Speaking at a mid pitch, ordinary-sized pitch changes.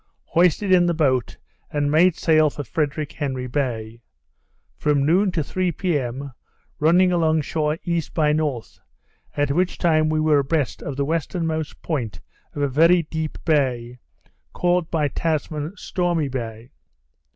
Yes: medium, 155 Hz; average, 3.0 semitones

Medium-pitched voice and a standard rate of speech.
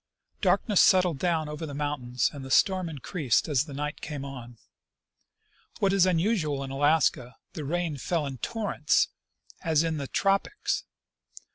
Yes: medium, 150 Hz; average, 155 wpm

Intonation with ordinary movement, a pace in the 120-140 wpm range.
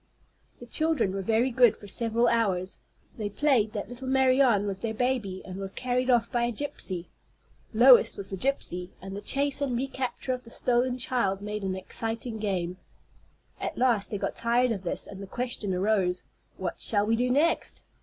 No: average, 4.4 semitones; average, 185 wpm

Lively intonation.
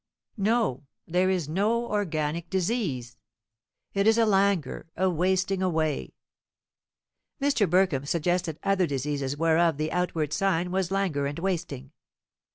No: average, 4.1 semitones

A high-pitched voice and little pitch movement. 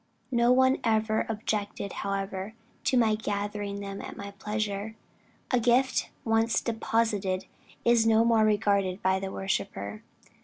Yes: high, 215 Hz; narrow, 2.2 semitones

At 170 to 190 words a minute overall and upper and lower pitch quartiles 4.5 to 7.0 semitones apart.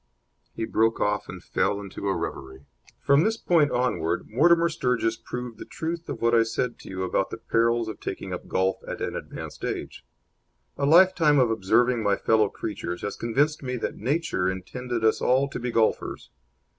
Yes: average, 185 wpm; average, 5.1 semitones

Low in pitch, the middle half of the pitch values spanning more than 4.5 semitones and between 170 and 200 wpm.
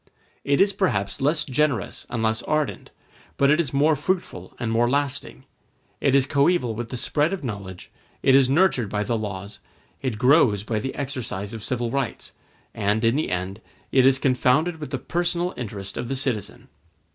Yes: low, 130 Hz; average, 4.9 semitones; average, 180 wpm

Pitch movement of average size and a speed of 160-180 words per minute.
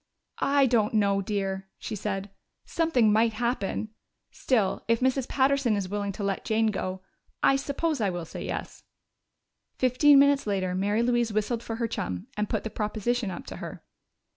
Yes: average, 3.8 semitones; average, 170 wpm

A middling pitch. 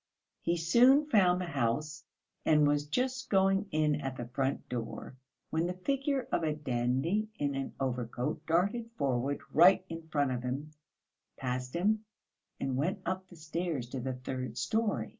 Yes: medium, 155 Hz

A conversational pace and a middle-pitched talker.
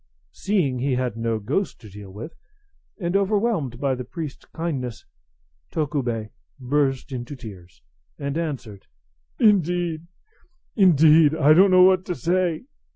No: slow, 130 wpm; medium, 145 Hz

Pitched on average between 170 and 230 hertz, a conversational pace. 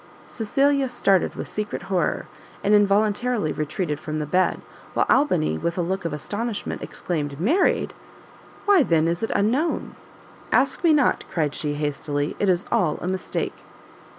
Yes: medium, 185 Hz; average, 150 wpm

